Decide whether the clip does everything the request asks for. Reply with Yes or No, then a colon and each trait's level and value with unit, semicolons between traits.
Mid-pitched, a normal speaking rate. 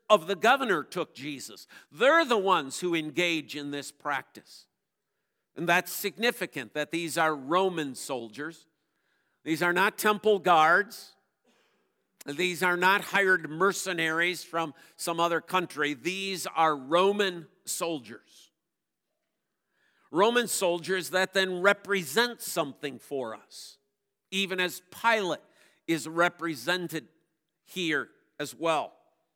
No: medium, 175 Hz; slow, 110 wpm